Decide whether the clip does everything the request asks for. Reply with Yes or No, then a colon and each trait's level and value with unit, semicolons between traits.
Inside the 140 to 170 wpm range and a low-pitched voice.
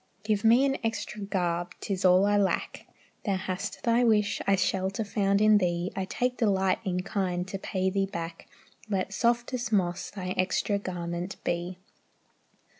No: average, 160 wpm; high, 195 Hz